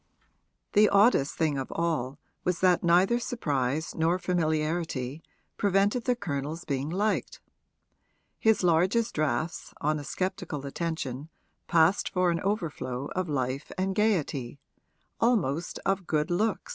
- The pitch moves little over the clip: No, average, 4.9 semitones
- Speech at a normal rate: No, slow, 125 wpm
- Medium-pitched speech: Yes, medium, 170 Hz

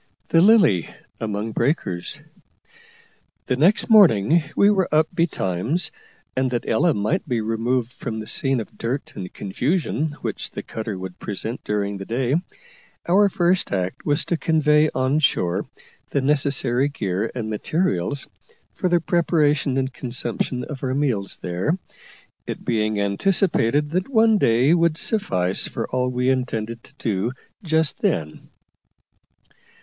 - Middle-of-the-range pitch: No, low, 130 Hz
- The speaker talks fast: No, average, 140 wpm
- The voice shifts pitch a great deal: Yes, wide, 6.6 semitones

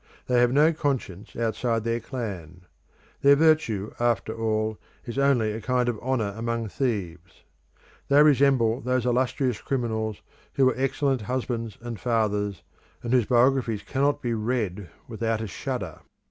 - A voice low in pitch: Yes, low, 120 Hz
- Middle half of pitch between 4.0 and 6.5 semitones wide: No, average, 3.1 semitones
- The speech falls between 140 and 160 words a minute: Yes, average, 145 wpm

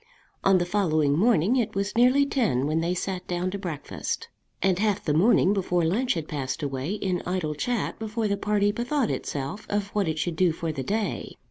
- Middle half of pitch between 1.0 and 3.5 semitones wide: No, average, 4.7 semitones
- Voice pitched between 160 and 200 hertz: Yes, high, 190 Hz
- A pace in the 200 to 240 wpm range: Yes, fast, 205 wpm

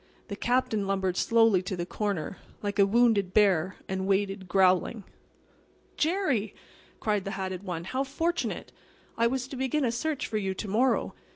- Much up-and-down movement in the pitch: No, average, 4.3 semitones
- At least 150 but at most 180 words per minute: Yes, average, 165 wpm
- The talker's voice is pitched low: No, high, 205 Hz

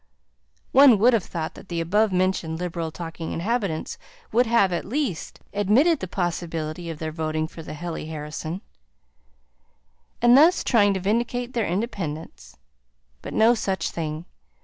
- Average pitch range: No, wide, 5.8 semitones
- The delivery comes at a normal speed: Yes, average, 150 wpm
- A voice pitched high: No, medium, 180 Hz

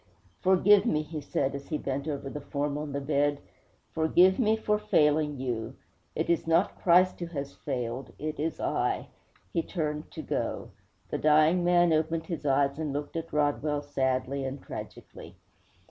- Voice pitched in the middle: Yes, medium, 150 Hz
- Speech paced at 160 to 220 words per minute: Yes, average, 170 wpm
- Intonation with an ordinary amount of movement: Yes, average, 3.0 semitones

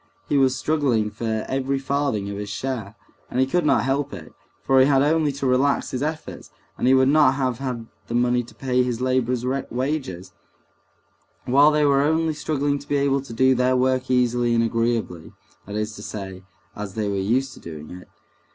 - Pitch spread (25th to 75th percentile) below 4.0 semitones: Yes, average, 3.3 semitones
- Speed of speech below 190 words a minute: No, average, 200 wpm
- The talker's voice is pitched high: No, low, 130 Hz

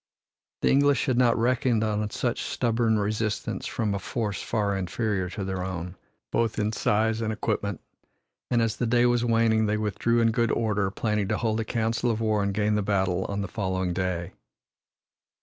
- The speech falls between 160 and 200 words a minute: Yes, average, 185 wpm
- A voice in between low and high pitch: No, low, 110 Hz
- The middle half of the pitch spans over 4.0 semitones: No, narrow, 2.5 semitones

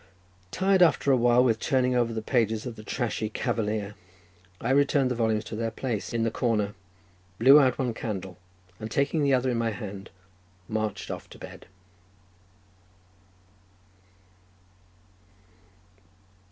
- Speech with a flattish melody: No, average, 3.0 semitones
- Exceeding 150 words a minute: No, average, 140 wpm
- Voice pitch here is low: Yes, low, 115 Hz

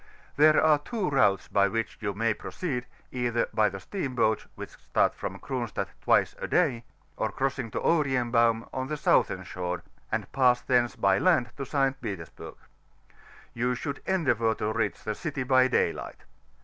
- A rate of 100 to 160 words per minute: No, average, 170 wpm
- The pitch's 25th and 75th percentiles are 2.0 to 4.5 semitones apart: Yes, average, 3.7 semitones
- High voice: No, low, 125 Hz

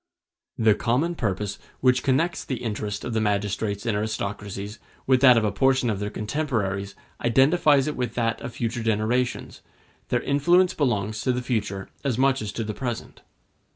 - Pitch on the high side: No, low, 115 Hz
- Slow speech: No, average, 170 wpm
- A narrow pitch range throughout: No, average, 3.9 semitones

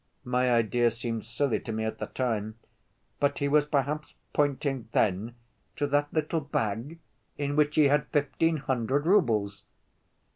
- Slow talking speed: No, average, 150 wpm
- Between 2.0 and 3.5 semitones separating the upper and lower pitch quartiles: No, average, 4.2 semitones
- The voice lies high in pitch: No, low, 135 Hz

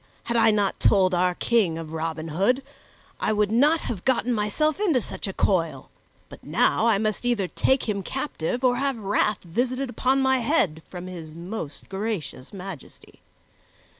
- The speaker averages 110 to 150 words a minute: No, average, 165 wpm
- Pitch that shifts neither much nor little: No, wide, 5.7 semitones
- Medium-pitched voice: No, high, 210 Hz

